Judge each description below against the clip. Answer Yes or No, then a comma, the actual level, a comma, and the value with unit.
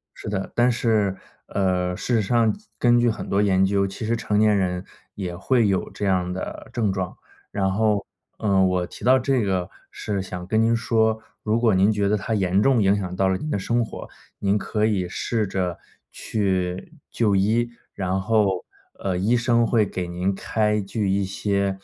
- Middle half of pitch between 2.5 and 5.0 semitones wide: Yes, average, 2.8 semitones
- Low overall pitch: Yes, low, 100 Hz